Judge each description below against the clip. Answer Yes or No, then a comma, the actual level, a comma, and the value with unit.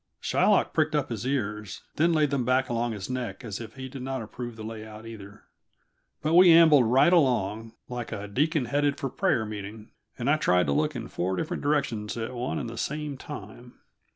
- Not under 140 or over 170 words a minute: No, fast, 205 wpm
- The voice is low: Yes, low, 120 Hz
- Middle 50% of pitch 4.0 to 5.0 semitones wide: Yes, average, 4.6 semitones